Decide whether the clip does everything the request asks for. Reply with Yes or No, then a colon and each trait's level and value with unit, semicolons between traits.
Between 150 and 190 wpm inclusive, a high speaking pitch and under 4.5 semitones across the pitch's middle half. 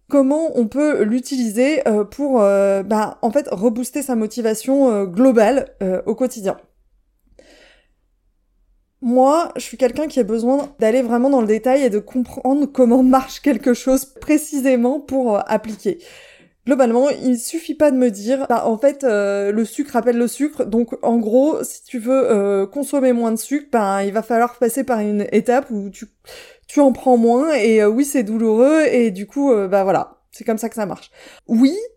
Yes: average, 185 wpm; high, 245 Hz; average, 3.7 semitones